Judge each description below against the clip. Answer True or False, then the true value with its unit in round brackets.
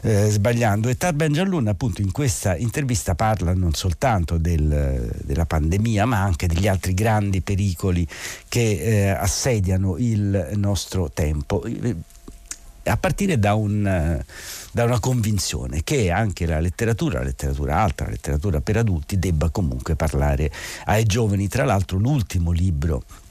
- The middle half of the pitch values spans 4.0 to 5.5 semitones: True (4.5 semitones)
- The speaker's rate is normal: True (140 wpm)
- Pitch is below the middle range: True (100 Hz)